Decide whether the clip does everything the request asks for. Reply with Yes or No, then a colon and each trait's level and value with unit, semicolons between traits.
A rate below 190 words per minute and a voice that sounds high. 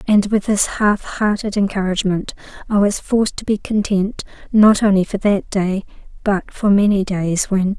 Yes: average, 170 wpm; high, 200 Hz